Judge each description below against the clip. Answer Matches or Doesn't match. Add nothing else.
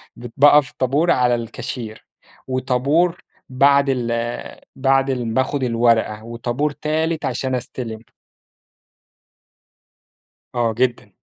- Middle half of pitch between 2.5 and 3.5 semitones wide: Matches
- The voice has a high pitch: Doesn't match